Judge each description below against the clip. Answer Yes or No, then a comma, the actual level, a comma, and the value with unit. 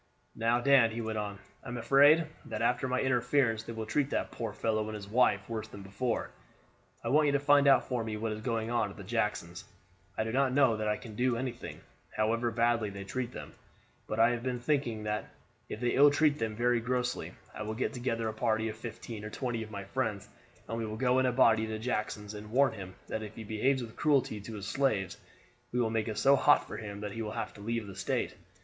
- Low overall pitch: Yes, low, 115 Hz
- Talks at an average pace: No, fast, 240 wpm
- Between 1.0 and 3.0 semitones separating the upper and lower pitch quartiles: Yes, average, 2.7 semitones